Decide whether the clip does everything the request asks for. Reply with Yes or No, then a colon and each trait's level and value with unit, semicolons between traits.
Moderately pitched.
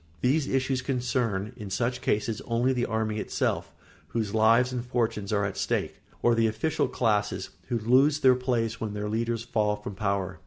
No: low, 115 Hz